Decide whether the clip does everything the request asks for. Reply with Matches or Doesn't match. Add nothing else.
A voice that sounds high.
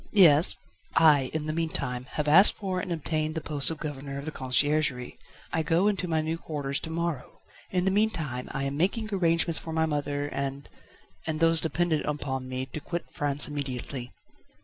Doesn't match